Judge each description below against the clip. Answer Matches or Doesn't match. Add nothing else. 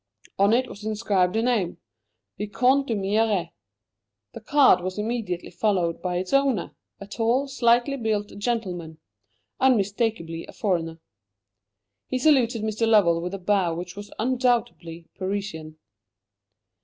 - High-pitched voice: Matches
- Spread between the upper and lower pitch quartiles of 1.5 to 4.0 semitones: Doesn't match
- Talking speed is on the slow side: Matches